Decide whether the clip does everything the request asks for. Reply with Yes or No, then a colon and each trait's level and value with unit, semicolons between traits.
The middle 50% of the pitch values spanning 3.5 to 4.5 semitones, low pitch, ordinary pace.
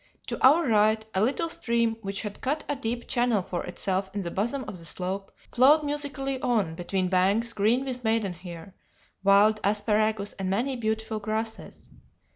No: average, 3.8 semitones; high, 220 Hz; average, 165 wpm